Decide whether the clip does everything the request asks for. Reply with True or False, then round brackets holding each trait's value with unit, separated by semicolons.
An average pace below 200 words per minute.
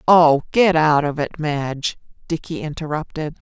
True (135 wpm)